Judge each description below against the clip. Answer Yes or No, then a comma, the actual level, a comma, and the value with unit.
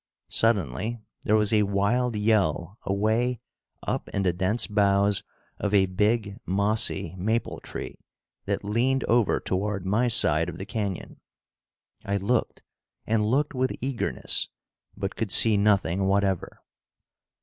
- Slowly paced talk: Yes, slow, 130 wpm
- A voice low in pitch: Yes, low, 105 Hz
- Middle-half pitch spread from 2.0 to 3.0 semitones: Yes, narrow, 2.6 semitones